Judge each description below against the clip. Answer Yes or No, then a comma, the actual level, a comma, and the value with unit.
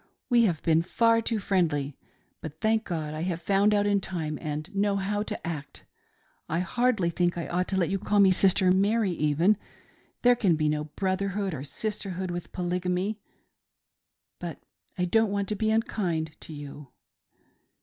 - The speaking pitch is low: No, medium, 185 Hz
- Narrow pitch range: No, average, 4.0 semitones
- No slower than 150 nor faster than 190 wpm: Yes, average, 180 wpm